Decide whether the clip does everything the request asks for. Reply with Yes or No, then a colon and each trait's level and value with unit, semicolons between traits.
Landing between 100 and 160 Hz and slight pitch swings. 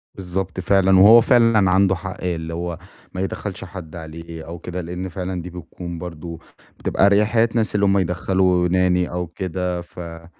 No: very low, 90 Hz; narrow, 1.9 semitones